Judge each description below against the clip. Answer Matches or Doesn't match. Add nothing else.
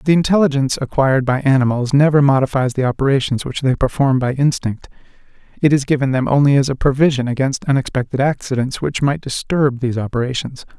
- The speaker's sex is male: Matches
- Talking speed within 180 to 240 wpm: Doesn't match